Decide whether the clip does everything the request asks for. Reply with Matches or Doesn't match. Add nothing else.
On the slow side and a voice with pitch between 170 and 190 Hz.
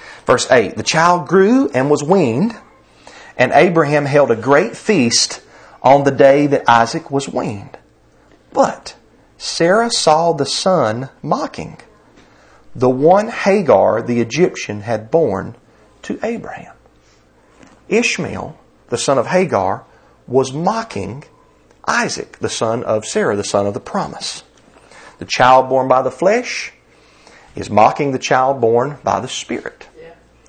Doesn't match